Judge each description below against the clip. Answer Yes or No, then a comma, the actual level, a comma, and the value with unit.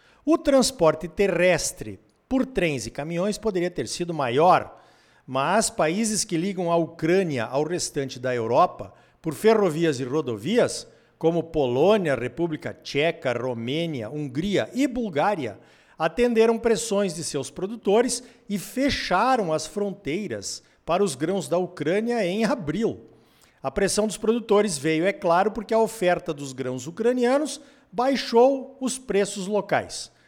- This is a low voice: No, medium, 180 Hz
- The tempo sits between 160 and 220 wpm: No, average, 130 wpm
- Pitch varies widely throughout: Yes, wide, 6.2 semitones